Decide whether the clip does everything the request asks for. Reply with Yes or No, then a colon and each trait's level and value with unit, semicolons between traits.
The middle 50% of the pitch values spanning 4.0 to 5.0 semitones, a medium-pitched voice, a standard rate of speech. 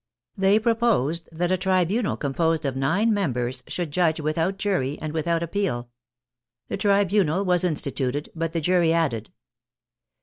Yes: average, 4.5 semitones; medium, 170 Hz; average, 145 wpm